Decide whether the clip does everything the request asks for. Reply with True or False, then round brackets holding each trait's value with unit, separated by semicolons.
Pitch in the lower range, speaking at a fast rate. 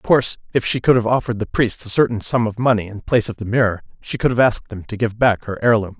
True (110 Hz; 290 wpm)